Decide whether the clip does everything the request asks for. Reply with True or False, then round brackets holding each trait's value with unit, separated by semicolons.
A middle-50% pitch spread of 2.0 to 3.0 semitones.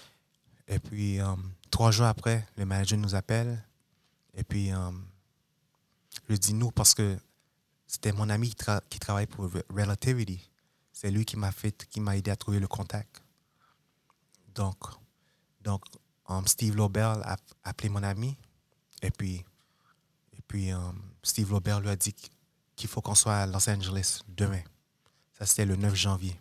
True (2.7 semitones)